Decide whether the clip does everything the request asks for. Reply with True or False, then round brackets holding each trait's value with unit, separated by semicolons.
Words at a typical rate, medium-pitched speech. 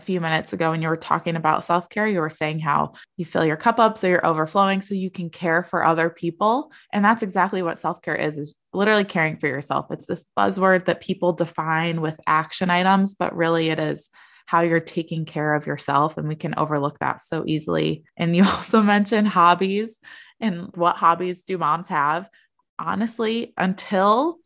True (190 wpm; 175 Hz)